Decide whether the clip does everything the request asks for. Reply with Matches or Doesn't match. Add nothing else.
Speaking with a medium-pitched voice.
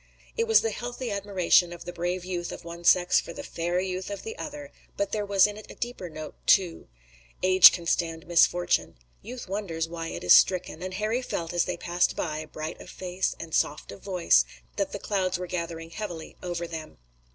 Matches